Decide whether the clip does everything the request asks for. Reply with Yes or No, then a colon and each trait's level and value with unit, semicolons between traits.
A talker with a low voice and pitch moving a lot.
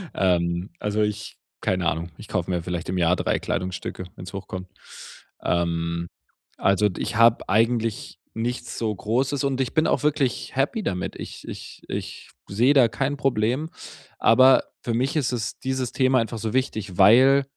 Yes: low, 110 Hz; wide, 5.9 semitones